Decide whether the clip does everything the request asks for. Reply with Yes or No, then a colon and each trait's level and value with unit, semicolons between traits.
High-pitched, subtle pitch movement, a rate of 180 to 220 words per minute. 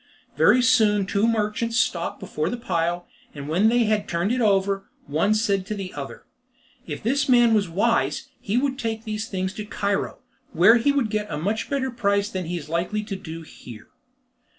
No: high, 210 Hz; average, 3.6 semitones; average, 195 wpm